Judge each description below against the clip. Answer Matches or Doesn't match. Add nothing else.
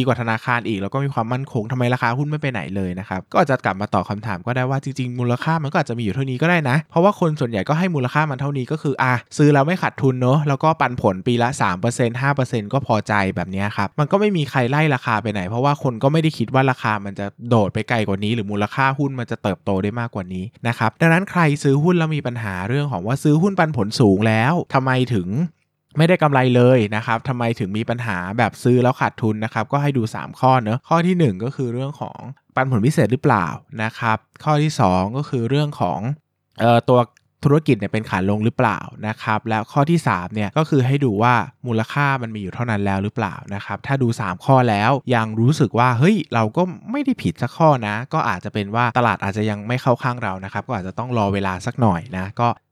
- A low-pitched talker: Matches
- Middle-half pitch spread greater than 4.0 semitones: Matches